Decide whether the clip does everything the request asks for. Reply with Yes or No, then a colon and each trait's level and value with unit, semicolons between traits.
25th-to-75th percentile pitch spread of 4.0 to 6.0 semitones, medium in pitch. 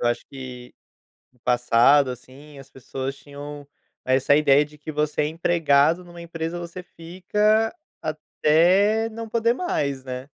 Yes: average, 4.3 semitones; medium, 150 Hz